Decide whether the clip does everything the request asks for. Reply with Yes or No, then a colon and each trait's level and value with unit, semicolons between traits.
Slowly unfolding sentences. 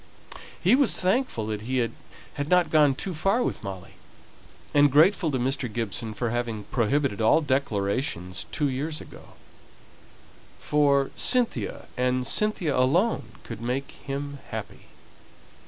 Yes: slow, 130 wpm